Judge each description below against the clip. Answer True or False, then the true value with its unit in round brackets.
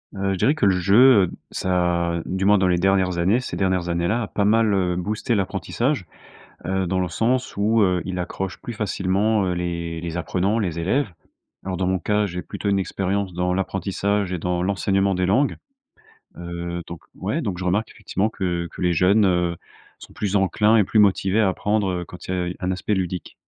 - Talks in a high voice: False (95 Hz)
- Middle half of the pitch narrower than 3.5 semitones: True (2.5 semitones)